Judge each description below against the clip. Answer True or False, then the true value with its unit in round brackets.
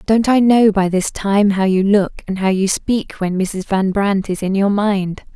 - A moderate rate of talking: False (235 wpm)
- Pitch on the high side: True (200 Hz)